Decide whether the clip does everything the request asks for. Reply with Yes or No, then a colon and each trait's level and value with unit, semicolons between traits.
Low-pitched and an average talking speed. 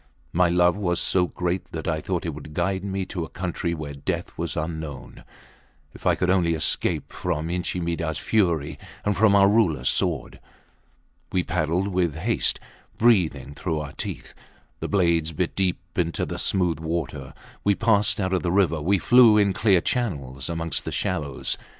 Yes: very low, 85 Hz; average, 175 wpm